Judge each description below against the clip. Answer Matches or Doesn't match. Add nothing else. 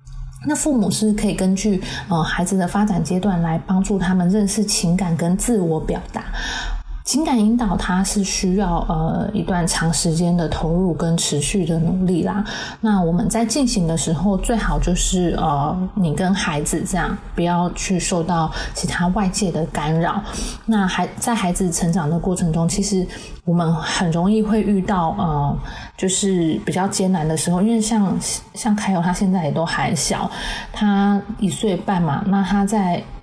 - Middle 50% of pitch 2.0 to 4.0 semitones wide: Matches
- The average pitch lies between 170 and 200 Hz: Matches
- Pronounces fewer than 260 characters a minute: Matches